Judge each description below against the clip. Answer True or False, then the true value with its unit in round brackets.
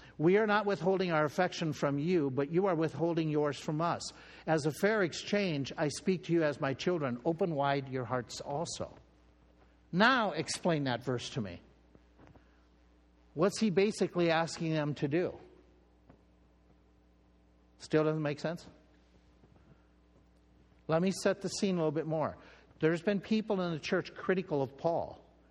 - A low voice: False (150 Hz)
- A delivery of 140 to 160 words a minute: True (155 wpm)